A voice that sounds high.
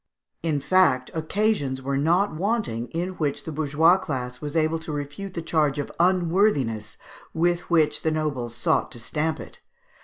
No: medium, 155 Hz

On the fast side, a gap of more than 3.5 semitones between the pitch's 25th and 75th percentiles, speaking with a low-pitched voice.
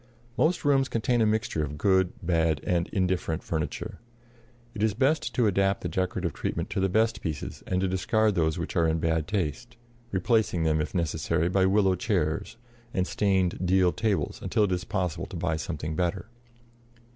No: average, 180 wpm; average, 4.3 semitones; very low, 90 Hz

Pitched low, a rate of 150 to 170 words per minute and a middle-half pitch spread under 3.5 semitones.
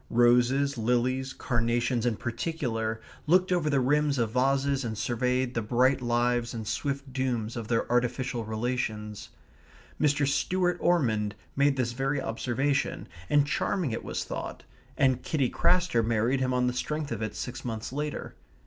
Yes: low, 125 Hz; average, 155 wpm; average, 3.0 semitones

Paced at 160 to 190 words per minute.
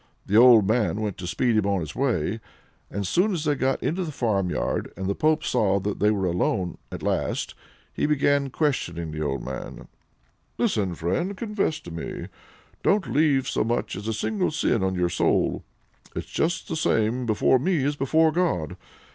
Yes: average, 180 wpm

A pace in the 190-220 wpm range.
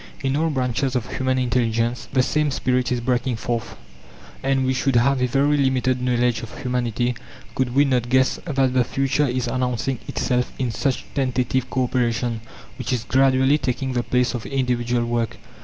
No: average, 175 wpm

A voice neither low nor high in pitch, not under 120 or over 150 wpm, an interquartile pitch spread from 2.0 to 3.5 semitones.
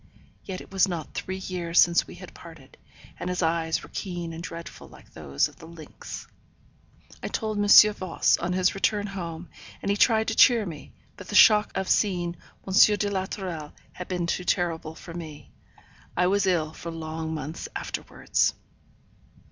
No: medium, 180 Hz; average, 180 wpm; average, 3.0 semitones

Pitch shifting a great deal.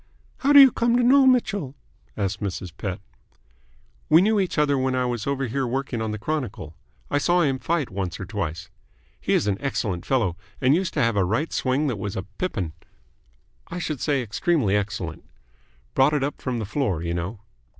Yes: wide, 7.2 semitones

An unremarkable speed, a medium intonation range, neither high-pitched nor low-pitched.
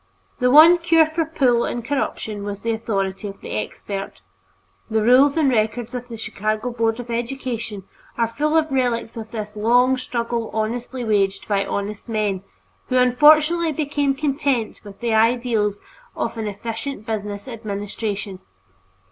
No: average, 150 wpm; average, 3.7 semitones; high, 230 Hz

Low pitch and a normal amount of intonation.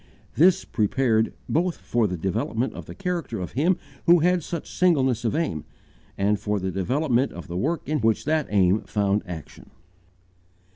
No: low, 120 Hz; wide, 7.9 semitones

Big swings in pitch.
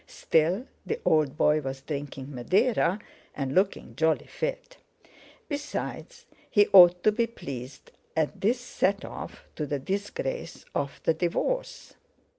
Yes: wide, 8.8 semitones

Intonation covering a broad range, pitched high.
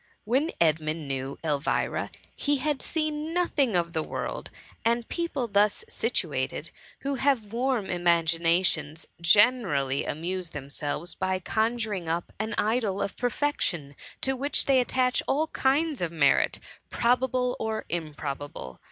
Yes: wide, 7.8 semitones; high, 205 Hz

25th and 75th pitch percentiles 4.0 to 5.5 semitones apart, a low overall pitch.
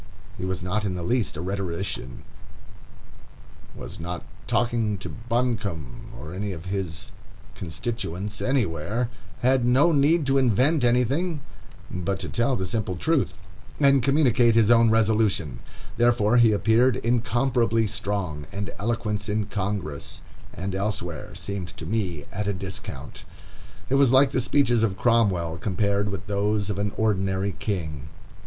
Yes: average, 4.3 semitones; low, 105 Hz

